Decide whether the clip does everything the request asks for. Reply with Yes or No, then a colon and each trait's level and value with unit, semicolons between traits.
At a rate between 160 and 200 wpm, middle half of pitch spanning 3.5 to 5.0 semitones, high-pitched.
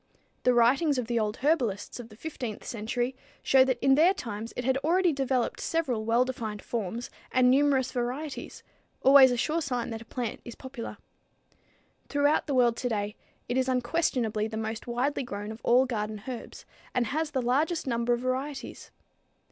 No: average, 175 wpm; average, 2.8 semitones; very high, 250 Hz